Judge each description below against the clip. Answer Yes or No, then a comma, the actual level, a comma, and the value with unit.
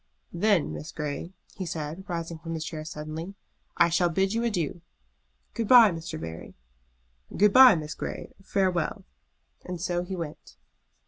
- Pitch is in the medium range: Yes, medium, 170 Hz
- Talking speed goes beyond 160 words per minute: No, average, 150 wpm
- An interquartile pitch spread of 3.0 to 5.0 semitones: Yes, average, 3.3 semitones